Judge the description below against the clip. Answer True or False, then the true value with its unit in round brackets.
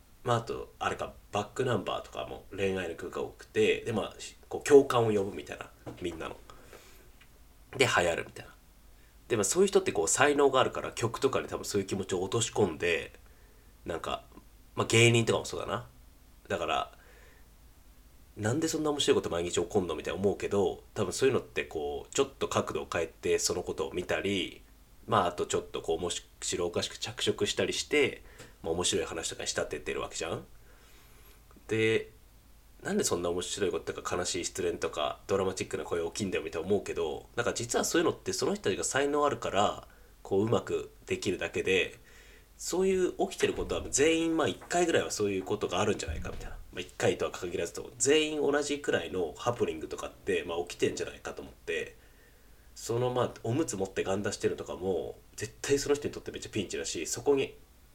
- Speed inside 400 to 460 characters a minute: True (420 characters per minute)